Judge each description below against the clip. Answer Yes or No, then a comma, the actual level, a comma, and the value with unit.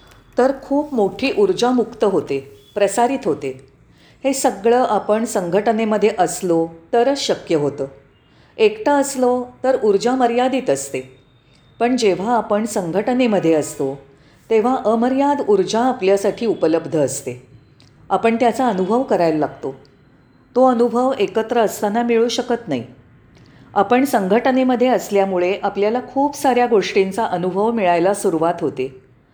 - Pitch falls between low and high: No, high, 210 Hz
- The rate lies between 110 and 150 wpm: Yes, average, 115 wpm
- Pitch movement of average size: No, wide, 7.7 semitones